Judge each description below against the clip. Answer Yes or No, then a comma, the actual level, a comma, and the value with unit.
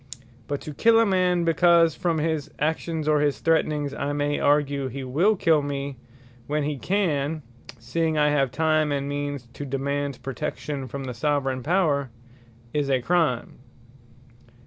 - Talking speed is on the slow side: No, average, 155 wpm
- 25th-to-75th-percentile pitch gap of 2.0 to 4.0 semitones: Yes, narrow, 2.6 semitones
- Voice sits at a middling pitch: Yes, medium, 145 Hz